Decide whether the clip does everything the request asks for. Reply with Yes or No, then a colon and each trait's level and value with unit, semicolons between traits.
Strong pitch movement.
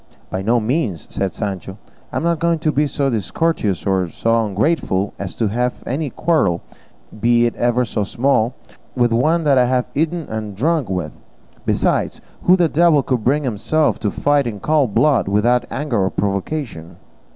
Yes: wide, 6.6 semitones